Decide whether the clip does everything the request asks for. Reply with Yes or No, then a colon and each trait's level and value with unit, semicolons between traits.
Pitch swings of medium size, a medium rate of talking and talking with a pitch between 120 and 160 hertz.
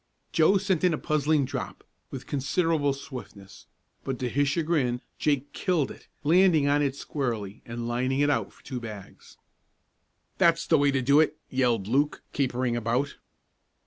Yes: average, 3.8 semitones; average, 160 wpm; medium, 140 Hz